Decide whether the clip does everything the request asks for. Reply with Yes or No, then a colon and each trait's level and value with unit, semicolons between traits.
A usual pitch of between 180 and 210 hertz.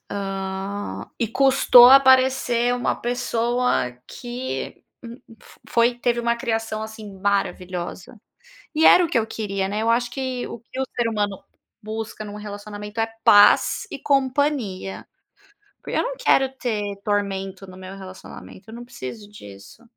No: high, 220 Hz